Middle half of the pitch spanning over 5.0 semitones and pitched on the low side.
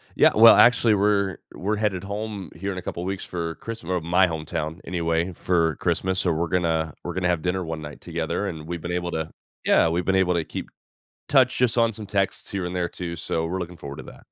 No: average, 2.8 semitones; very low, 90 Hz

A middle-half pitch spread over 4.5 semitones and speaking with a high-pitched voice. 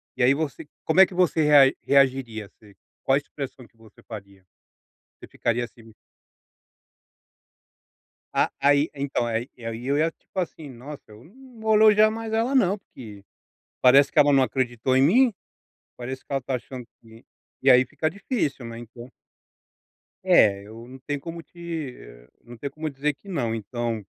No: average, 5.1 semitones; low, 135 Hz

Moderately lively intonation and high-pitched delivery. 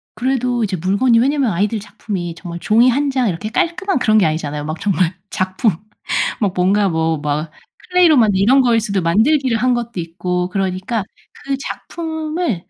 No: wide, 6.0 semitones; high, 210 Hz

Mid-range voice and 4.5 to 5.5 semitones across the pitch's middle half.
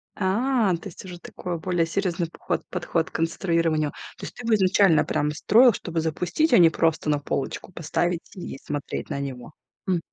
No: medium, 170 Hz; average, 3.0 semitones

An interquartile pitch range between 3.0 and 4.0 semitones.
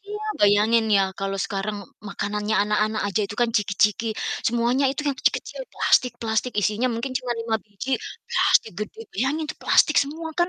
Yes: average, 3.7 semitones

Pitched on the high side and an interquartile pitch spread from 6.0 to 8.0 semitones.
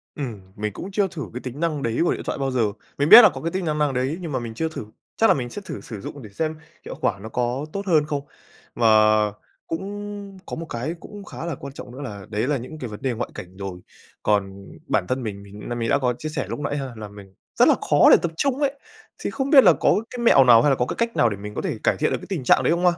No: low, 135 Hz; wide, 6.7 semitones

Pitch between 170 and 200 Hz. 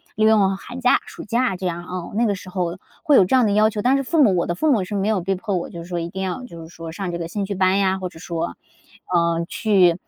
Yes: high, 190 Hz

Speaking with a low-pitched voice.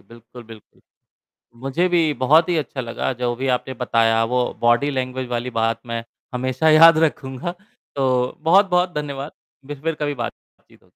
Yes: low, 130 Hz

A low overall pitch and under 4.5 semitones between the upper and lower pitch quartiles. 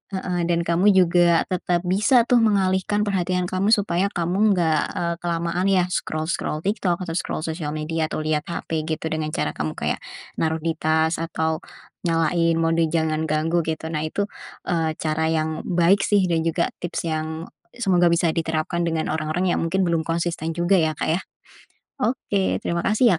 No: medium, 170 Hz; narrow, 2.4 semitones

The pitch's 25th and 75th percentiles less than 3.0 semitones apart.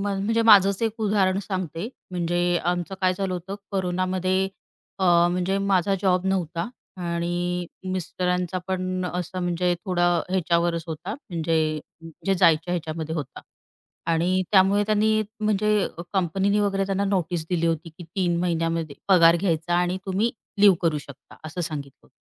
Yes: narrow, 2.4 semitones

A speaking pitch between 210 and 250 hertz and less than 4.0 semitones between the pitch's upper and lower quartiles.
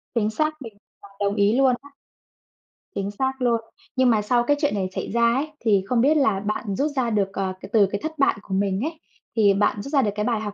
No: high, 225 Hz; average, 4.6 semitones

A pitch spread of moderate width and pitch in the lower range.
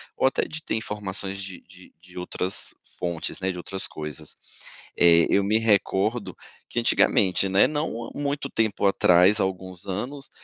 Yes: average, 3.5 semitones; very low, 95 Hz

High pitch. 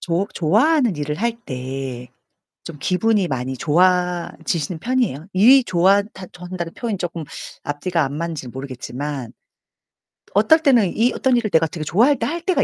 No: medium, 175 Hz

